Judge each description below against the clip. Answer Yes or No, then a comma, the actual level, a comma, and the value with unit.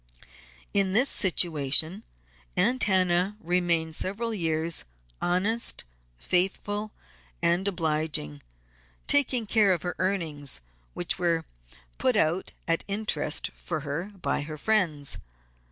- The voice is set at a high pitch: No, medium, 180 Hz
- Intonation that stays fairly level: No, average, 4.3 semitones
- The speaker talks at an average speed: No, slow, 105 wpm